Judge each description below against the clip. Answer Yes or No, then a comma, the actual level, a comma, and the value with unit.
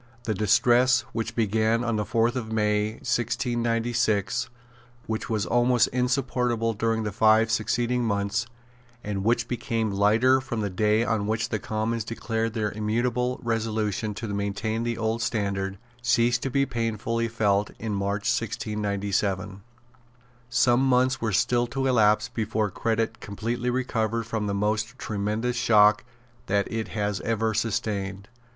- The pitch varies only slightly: Yes, narrow, 2.2 semitones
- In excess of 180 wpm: No, average, 140 wpm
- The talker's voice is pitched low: Yes, low, 110 Hz